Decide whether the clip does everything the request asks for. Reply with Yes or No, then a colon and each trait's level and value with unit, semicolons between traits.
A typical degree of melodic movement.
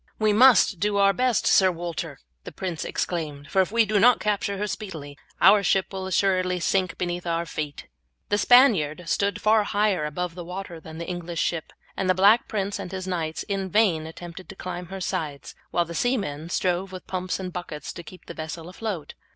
Yes: average, 3.0 semitones